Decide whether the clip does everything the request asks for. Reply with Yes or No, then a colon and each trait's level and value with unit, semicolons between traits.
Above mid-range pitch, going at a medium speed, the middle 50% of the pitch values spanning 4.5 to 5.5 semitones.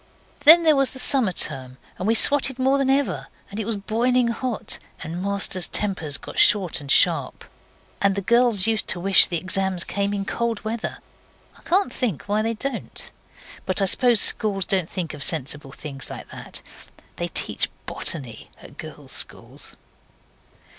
Yes: high, 200 Hz; average, 170 wpm; average, 5.2 semitones